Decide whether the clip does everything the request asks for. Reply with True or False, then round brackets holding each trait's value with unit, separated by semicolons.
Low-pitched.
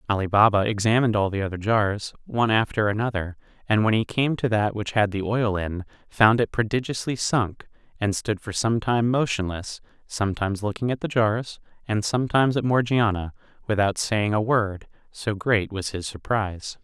True (110 Hz)